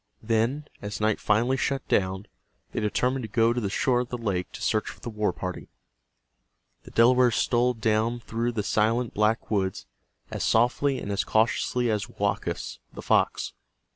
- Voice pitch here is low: Yes, low, 115 Hz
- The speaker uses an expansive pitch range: No, narrow, 2.6 semitones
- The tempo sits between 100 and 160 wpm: No, average, 170 wpm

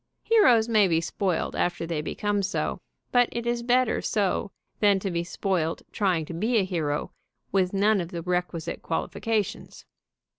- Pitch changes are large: No, average, 4.2 semitones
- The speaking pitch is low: No, high, 195 Hz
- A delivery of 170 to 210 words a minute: No, average, 160 wpm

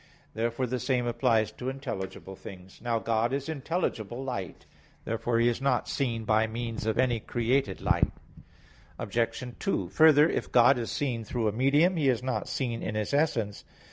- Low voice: Yes, low, 120 Hz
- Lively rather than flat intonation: No, average, 3.0 semitones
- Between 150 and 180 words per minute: Yes, average, 170 wpm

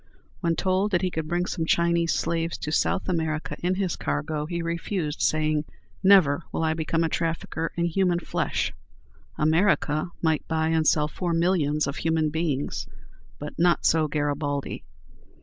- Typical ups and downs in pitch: No, narrow, 2.0 semitones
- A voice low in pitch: No, medium, 165 Hz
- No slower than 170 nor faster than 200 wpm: No, average, 160 wpm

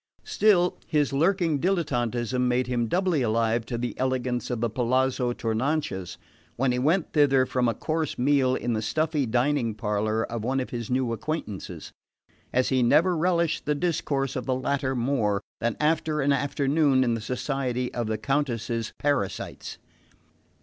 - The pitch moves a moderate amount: Yes, average, 3.8 semitones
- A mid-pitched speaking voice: No, low, 130 Hz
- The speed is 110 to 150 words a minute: No, average, 160 wpm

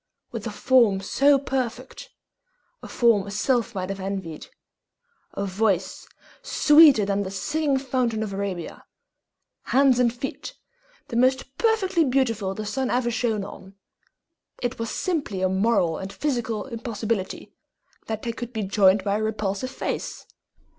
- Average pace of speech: Yes, average, 145 wpm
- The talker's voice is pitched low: No, high, 225 Hz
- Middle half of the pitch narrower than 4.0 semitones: No, average, 4.7 semitones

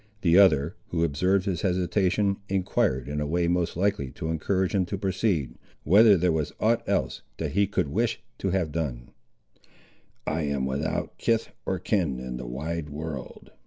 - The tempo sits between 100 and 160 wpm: No, average, 170 wpm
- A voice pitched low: Yes, very low, 85 Hz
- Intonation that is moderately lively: Yes, average, 4.8 semitones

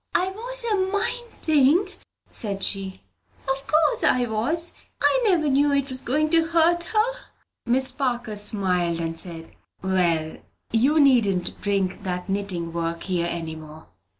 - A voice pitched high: Yes, high, 240 Hz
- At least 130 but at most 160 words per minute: Yes, average, 145 wpm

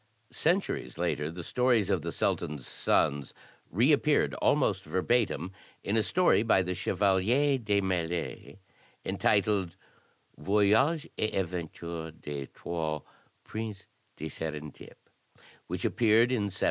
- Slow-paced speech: Yes, slow, 115 wpm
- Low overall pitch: Yes, very low, 95 Hz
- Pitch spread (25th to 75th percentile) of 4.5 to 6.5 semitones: Yes, wide, 5.5 semitones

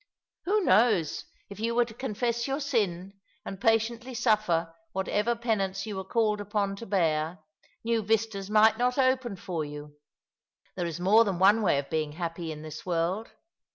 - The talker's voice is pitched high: Yes, high, 205 Hz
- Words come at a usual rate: Yes, average, 170 wpm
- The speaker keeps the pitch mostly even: No, average, 4.8 semitones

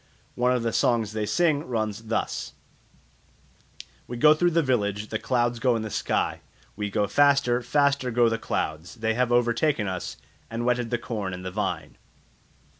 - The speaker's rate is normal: Yes, average, 175 wpm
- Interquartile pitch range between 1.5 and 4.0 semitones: Yes, average, 2.8 semitones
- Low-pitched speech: Yes, low, 120 Hz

